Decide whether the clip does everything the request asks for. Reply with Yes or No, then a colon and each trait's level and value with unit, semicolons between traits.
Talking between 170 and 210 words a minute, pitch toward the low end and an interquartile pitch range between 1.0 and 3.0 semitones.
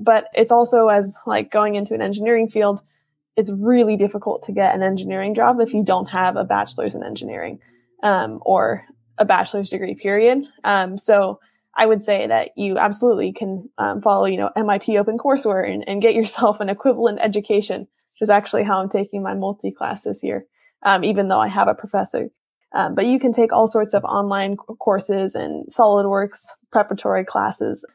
No: average, 185 wpm; high, 205 Hz; narrow, 2.4 semitones